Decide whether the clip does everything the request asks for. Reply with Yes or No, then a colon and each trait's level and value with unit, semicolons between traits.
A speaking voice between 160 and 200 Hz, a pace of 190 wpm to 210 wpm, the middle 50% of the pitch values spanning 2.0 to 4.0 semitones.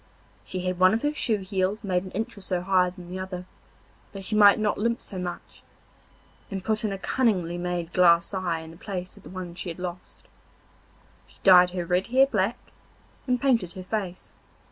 Yes: medium, 185 Hz; fast, 205 wpm; average, 2.7 semitones